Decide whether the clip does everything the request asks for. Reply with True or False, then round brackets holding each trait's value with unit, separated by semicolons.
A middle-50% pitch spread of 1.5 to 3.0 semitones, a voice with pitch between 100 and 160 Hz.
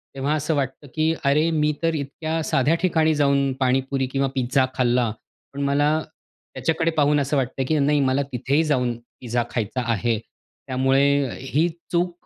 True (2.7 semitones; 140 Hz)